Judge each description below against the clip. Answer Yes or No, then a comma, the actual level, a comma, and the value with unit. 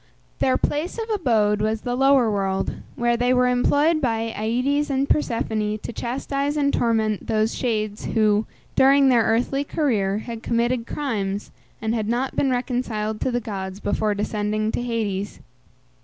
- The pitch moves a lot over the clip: No, average, 3.6 semitones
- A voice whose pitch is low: No, high, 230 Hz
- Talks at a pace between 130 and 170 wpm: Yes, average, 155 wpm